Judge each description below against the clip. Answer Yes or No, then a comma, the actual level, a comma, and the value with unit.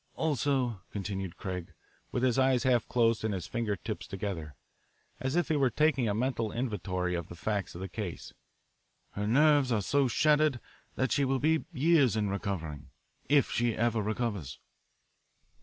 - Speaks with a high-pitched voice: No, low, 115 Hz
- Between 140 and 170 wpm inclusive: Yes, average, 165 wpm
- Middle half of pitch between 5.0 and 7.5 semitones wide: Yes, average, 5.3 semitones